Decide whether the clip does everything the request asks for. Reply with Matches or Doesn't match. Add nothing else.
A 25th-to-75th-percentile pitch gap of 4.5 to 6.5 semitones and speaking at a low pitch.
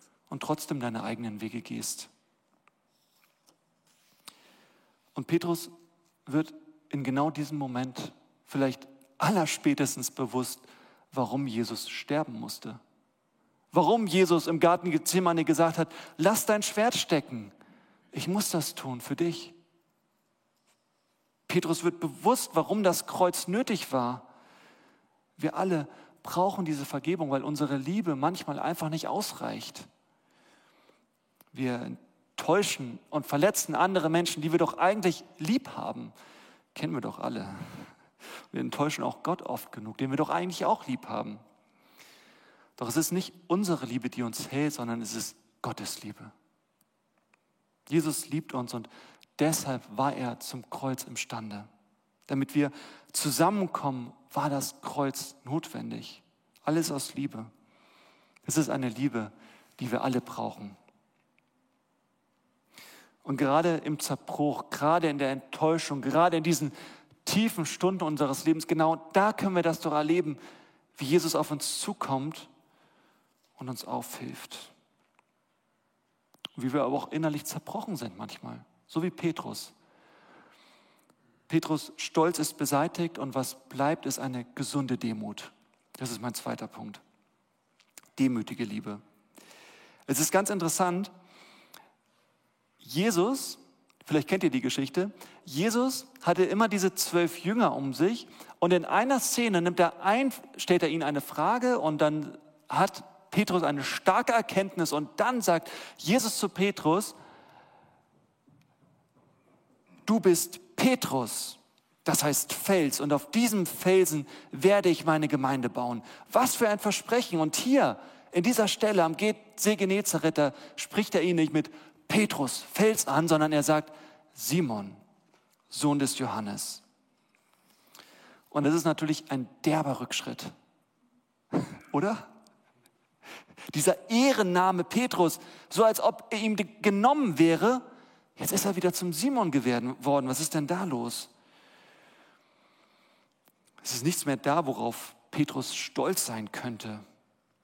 Doesn't match